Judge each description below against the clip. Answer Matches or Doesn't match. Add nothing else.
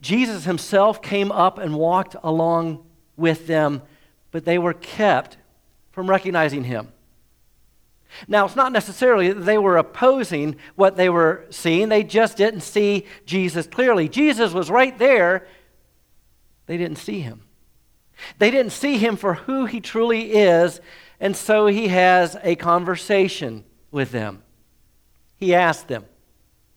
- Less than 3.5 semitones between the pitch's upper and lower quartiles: Doesn't match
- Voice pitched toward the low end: Doesn't match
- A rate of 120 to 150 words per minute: Matches